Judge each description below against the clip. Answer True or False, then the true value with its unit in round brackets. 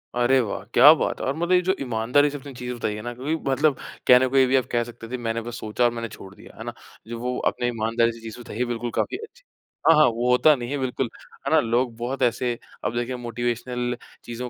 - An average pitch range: False (2.1 semitones)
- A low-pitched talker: True (120 Hz)